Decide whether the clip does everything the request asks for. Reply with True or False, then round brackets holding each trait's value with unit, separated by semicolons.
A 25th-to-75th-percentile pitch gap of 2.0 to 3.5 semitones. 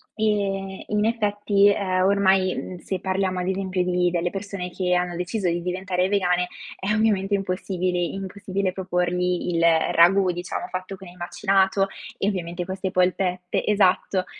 False (1.6 semitones)